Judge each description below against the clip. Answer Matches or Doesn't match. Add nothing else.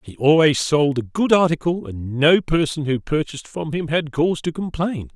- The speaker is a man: Matches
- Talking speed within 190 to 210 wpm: Matches